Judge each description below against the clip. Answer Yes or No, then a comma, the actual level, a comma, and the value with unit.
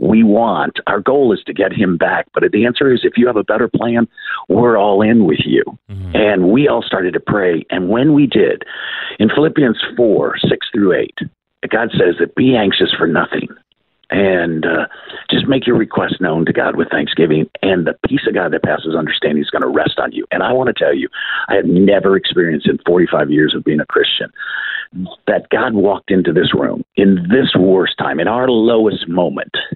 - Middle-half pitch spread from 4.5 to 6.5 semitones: Yes, average, 4.9 semitones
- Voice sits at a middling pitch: No, low, 110 Hz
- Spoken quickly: Yes, fast, 210 wpm